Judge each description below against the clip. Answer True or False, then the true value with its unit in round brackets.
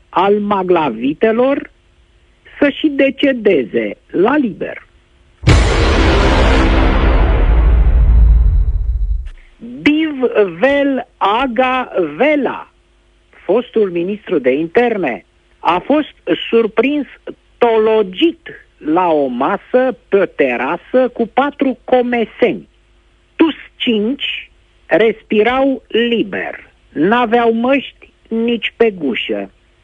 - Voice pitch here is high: True (225 Hz)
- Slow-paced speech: True (70 wpm)